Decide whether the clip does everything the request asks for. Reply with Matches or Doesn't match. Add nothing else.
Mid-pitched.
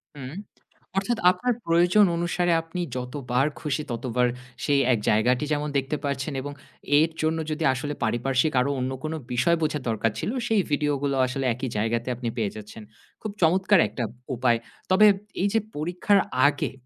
Matches